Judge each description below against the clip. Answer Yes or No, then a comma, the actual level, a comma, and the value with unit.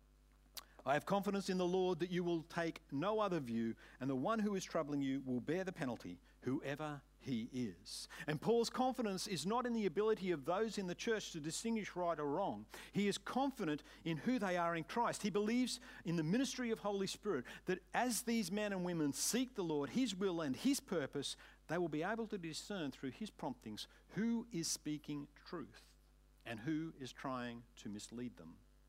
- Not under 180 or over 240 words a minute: Yes, average, 200 wpm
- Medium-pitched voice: Yes, medium, 180 Hz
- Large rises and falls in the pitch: Yes, wide, 6.5 semitones